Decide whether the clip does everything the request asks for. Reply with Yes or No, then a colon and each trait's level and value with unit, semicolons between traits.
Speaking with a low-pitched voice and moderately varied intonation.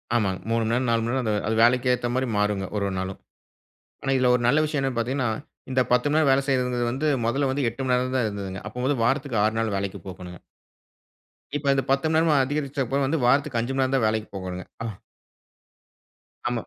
Yes: low, 125 Hz; average, 3.5 semitones